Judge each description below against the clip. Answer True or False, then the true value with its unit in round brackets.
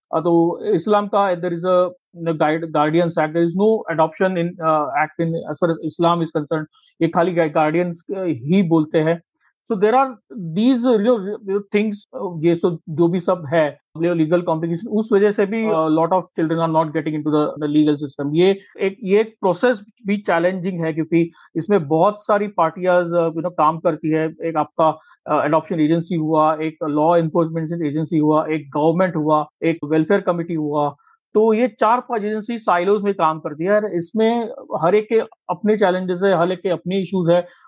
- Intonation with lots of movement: False (3.9 semitones)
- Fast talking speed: False (130 wpm)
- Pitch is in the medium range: True (170 Hz)